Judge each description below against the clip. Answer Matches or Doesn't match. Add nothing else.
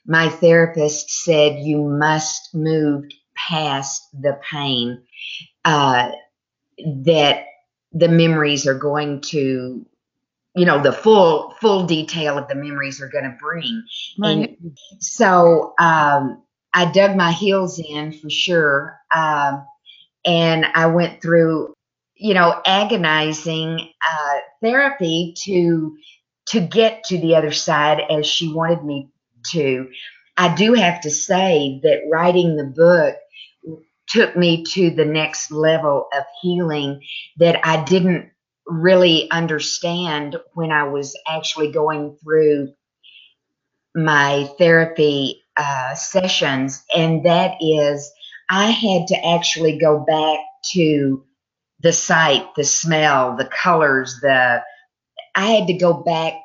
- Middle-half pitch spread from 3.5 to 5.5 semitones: Doesn't match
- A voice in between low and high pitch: Matches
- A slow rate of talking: Matches